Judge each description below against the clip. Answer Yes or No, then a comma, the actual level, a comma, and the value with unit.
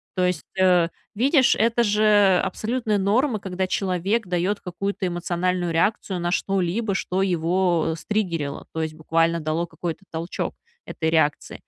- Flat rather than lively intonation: No, average, 3.4 semitones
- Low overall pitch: No, medium, 185 Hz